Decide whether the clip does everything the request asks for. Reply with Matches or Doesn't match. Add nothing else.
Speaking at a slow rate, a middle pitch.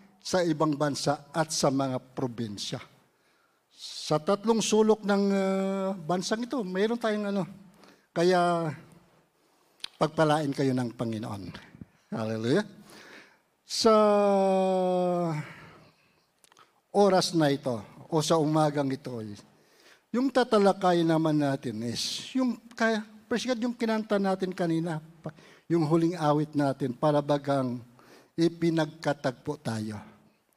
Matches